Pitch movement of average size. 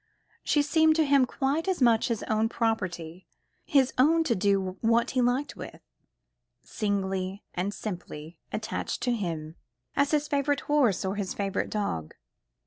No: wide, 6.6 semitones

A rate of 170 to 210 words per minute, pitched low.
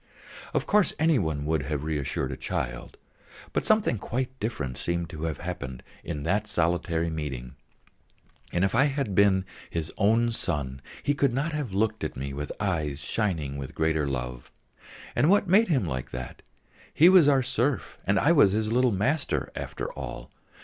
Yes: average, 175 wpm; very low, 95 Hz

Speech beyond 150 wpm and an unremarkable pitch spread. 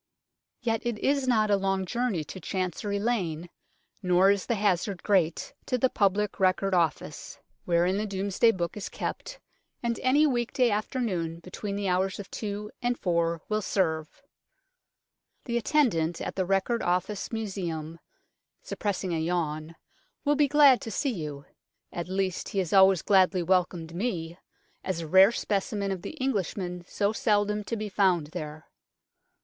Yes: average, 165 wpm; average, 3.6 semitones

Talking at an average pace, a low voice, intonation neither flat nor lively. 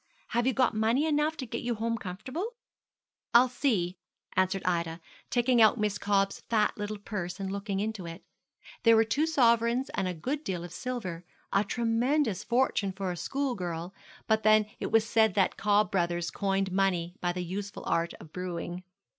No: average, 180 wpm; high, 205 Hz; average, 4.4 semitones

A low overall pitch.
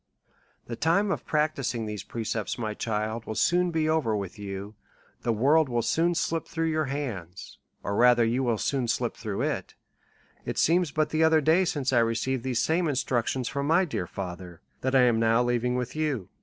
Yes: low, 125 Hz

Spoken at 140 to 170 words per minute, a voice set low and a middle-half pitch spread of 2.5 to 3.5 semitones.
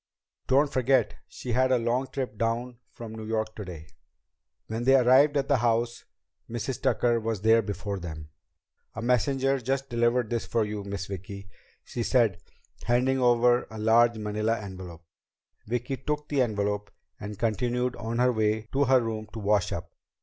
Yes: average, 165 wpm; low, 115 Hz; average, 2.9 semitones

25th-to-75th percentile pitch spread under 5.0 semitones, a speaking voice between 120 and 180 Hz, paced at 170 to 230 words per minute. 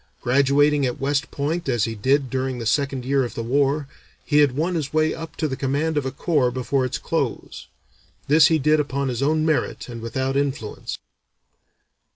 Yes: narrow, 2.5 semitones; medium, 140 Hz; average, 195 wpm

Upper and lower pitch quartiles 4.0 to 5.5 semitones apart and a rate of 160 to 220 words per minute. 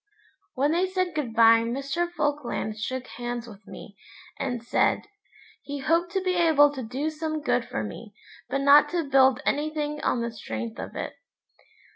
Yes: average, 4.6 semitones; average, 170 wpm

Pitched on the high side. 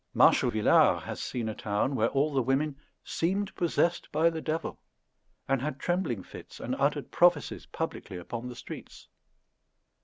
No: low, 135 Hz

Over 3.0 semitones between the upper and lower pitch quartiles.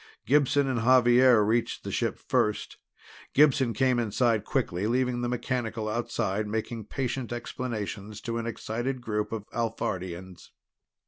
No: average, 2.7 semitones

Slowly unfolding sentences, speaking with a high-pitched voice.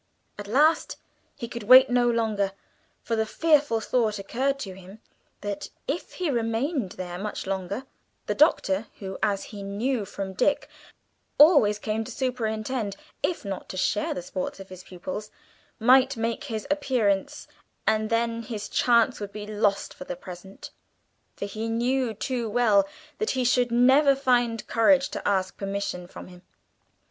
No: average, 160 wpm; high, 220 Hz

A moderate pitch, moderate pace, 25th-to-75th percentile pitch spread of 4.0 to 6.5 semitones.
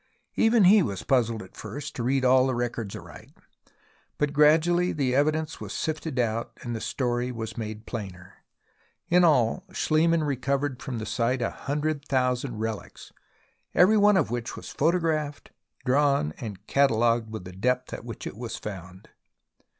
No: low, 130 Hz; average, 160 wpm; average, 4.8 semitones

